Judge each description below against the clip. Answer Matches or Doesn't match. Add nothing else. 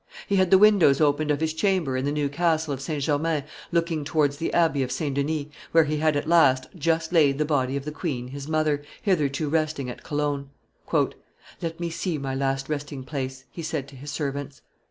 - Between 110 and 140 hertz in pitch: Doesn't match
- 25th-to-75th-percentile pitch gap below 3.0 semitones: Matches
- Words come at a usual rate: Doesn't match